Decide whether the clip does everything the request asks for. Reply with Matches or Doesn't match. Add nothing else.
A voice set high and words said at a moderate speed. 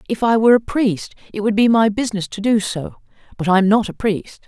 Doesn't match